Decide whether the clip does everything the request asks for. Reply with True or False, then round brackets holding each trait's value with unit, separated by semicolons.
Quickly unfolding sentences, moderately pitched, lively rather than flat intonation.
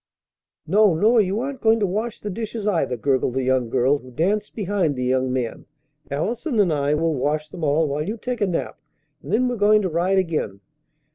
True (210 wpm; 170 Hz; 7.0 semitones)